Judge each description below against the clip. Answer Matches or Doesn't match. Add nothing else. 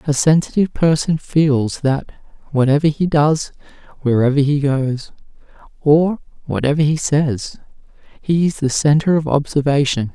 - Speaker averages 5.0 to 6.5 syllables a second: Doesn't match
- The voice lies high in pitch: Doesn't match